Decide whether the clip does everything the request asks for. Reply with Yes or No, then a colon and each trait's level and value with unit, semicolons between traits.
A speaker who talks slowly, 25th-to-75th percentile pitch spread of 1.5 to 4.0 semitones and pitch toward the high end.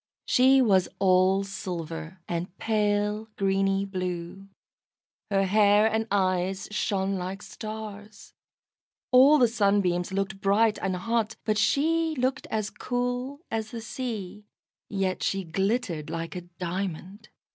Yes: slow, 125 wpm; average, 2.9 semitones; high, 200 Hz